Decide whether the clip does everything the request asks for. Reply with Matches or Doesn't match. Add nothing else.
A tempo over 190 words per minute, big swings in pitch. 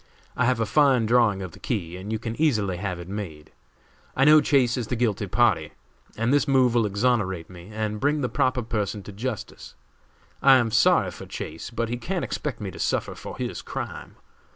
Doesn't match